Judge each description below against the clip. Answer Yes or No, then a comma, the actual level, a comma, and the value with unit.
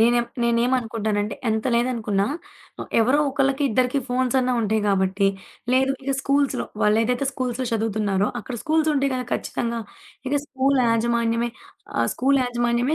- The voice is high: Yes, high, 240 Hz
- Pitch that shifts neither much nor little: Yes, average, 3.0 semitones